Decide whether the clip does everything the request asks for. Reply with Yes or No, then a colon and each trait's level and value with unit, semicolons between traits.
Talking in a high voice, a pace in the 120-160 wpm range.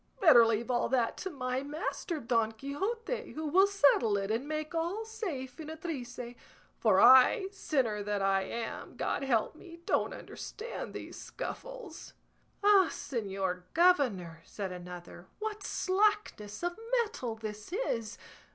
Yes: very high, 265 Hz; average, 140 wpm